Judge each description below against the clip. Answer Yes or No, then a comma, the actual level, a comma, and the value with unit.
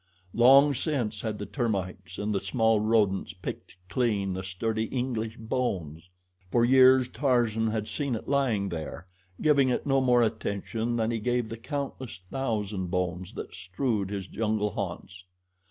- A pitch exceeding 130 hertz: No, low, 110 Hz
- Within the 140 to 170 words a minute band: Yes, average, 155 wpm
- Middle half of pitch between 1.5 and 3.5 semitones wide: No, average, 4.0 semitones